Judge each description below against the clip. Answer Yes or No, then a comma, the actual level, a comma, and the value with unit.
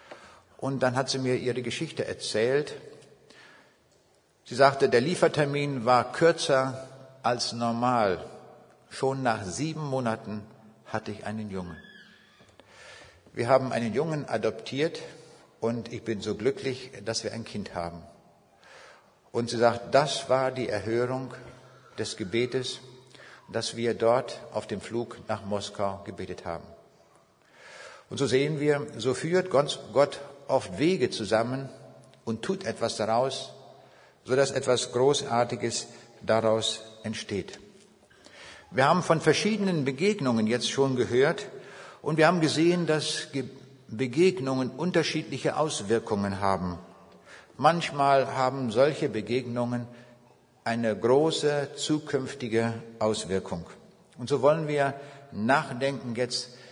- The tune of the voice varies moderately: Yes, average, 3.7 semitones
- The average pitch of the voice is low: Yes, low, 125 Hz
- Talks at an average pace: No, slow, 115 wpm